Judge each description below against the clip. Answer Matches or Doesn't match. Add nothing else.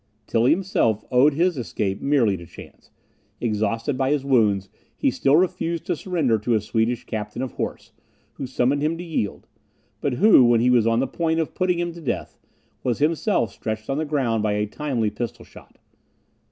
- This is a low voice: Matches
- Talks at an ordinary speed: Matches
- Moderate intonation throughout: Doesn't match